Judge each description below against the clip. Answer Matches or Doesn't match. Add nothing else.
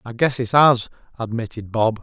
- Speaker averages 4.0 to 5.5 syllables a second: Matches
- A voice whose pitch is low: Matches